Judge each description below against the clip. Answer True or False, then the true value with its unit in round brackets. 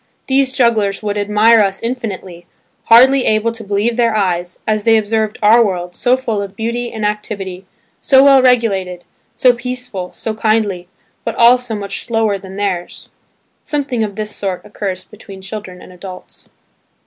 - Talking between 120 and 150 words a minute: False (160 wpm)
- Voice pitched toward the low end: False (215 Hz)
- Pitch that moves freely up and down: False (3.3 semitones)